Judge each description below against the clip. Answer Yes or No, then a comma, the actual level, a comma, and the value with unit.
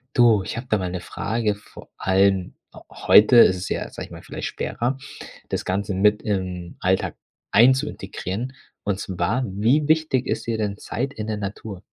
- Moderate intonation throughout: Yes, average, 3.8 semitones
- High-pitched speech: No, low, 105 Hz